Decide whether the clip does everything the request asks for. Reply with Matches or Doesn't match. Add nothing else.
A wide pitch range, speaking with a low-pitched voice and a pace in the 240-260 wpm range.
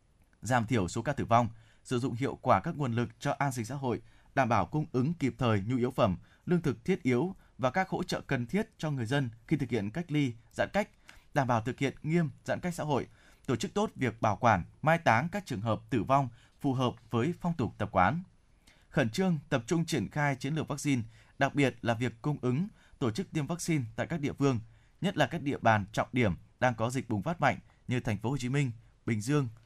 Doesn't match